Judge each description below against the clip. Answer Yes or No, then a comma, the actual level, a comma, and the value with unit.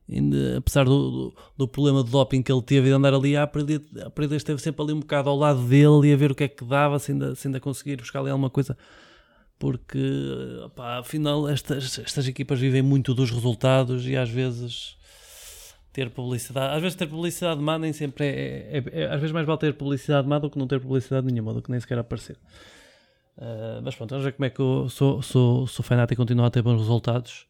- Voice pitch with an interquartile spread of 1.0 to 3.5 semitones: Yes, average, 2.8 semitones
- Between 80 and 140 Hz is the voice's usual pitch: Yes, low, 135 Hz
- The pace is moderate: No, fast, 225 wpm